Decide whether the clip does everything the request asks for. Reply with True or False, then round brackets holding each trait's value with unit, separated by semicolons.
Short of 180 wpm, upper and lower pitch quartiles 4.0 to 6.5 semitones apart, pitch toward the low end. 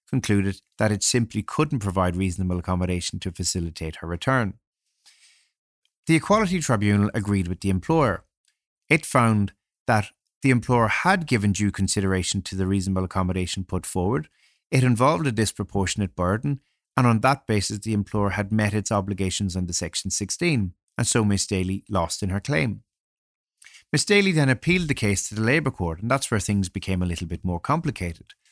True (170 wpm; 4.9 semitones; 100 Hz)